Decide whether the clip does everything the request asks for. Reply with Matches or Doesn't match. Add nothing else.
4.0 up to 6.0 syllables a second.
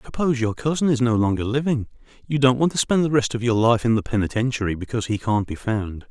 Doesn't match